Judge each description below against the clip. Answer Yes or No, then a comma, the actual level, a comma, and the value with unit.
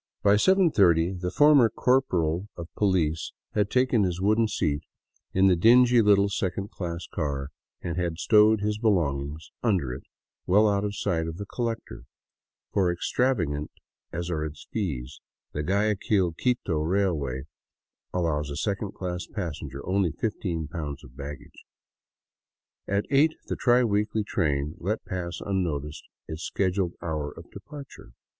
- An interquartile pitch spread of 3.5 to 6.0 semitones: Yes, average, 4.9 semitones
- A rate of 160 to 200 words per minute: No, average, 140 wpm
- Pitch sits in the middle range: No, very low, 90 Hz